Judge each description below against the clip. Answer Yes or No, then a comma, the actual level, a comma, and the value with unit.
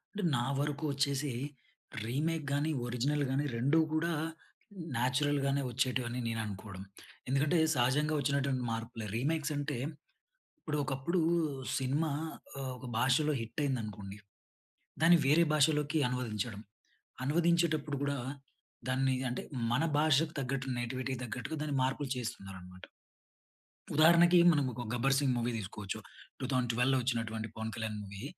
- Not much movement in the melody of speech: No, average, 3.8 semitones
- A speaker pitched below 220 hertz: Yes, low, 135 Hz